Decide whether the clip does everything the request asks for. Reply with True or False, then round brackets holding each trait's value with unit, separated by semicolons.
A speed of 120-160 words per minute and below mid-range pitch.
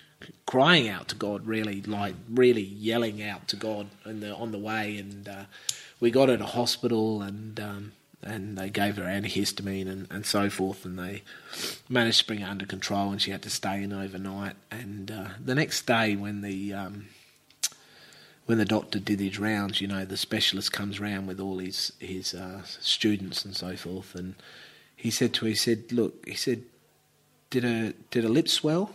False (195 wpm; 100 Hz)